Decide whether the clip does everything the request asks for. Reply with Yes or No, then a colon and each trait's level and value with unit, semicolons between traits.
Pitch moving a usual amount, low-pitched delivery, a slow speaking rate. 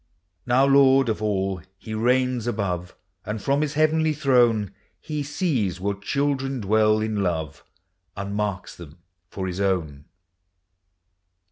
No: wide, 5.7 semitones; low, 110 Hz; slow, 130 wpm